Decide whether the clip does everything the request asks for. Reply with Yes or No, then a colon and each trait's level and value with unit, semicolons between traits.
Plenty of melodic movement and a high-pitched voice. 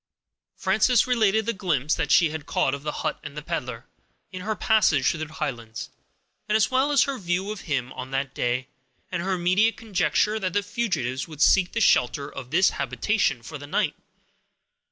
No: wide, 7.1 semitones; medium, 175 Hz